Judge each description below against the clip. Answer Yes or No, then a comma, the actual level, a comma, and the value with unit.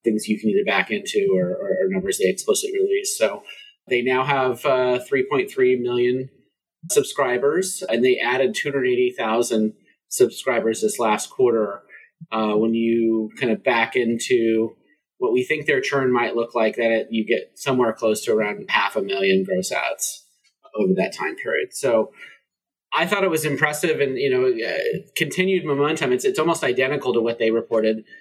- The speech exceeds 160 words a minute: Yes, average, 170 wpm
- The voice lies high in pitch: No, medium, 140 Hz